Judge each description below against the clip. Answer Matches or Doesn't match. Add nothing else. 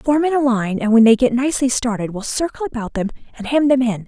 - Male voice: Doesn't match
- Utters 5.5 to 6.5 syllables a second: Matches